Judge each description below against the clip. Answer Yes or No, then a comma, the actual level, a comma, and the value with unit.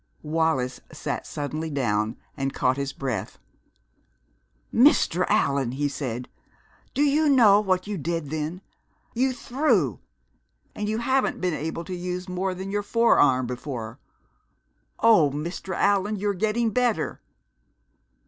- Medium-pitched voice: Yes, medium, 175 Hz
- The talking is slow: Yes, slow, 130 wpm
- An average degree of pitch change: No, wide, 7.1 semitones